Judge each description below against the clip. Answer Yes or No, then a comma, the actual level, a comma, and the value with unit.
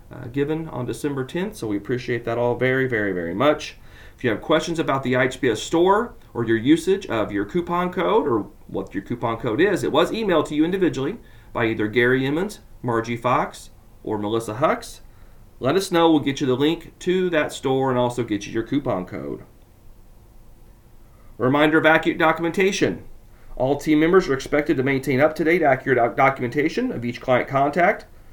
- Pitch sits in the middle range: No, low, 130 Hz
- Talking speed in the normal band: Yes, average, 190 wpm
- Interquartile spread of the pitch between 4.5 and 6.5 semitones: Yes, average, 5.1 semitones